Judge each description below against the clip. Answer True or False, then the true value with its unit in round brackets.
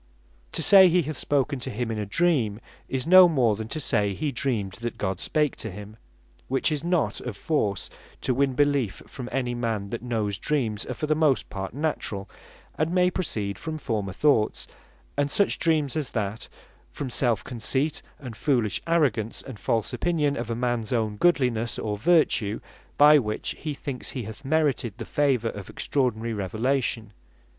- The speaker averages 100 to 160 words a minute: False (180 wpm)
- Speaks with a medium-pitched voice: False (125 Hz)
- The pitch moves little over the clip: False (5.3 semitones)